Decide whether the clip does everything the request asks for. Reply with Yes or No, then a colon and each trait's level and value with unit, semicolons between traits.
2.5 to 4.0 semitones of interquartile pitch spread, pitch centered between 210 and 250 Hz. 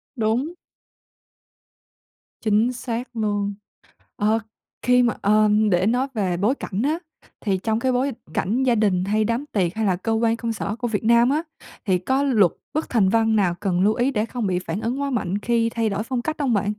Yes: average, 3.3 semitones; high, 225 Hz